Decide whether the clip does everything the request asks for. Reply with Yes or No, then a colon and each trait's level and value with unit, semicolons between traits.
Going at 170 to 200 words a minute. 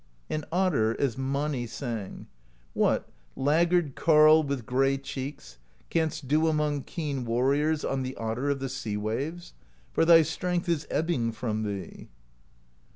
No: average, 140 wpm